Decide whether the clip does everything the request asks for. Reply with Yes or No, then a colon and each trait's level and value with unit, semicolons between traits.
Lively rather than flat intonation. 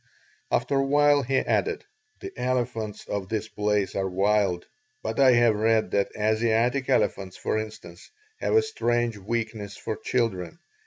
No: average, 3.4 semitones